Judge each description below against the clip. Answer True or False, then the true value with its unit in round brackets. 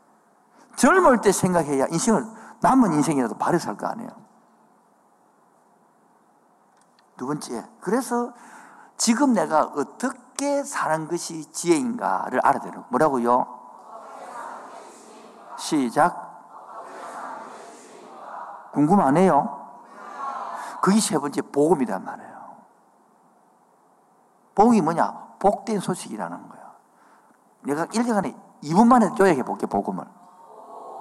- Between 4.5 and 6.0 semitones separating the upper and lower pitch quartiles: True (5.1 semitones)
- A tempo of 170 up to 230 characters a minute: True (205 characters per minute)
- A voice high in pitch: True (220 Hz)